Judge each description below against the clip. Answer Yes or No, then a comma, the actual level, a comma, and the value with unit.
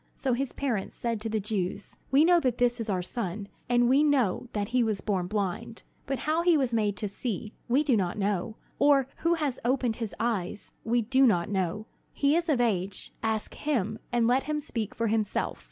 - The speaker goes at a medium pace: No, fast, 210 wpm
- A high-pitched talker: Yes, high, 230 Hz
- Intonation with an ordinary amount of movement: Yes, average, 4.4 semitones